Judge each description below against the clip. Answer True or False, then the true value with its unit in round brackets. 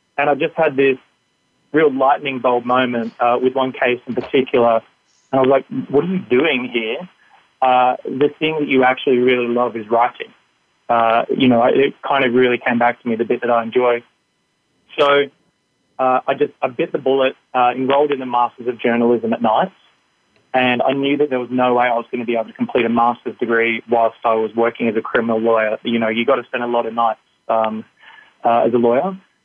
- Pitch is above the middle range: False (125 Hz)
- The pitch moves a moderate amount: False (2.2 semitones)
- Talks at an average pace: False (220 wpm)